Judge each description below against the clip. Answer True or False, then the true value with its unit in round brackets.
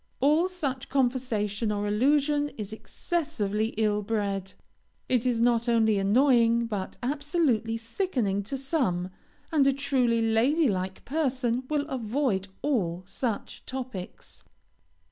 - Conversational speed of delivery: False (120 wpm)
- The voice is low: False (235 Hz)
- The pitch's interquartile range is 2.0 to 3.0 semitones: False (4.8 semitones)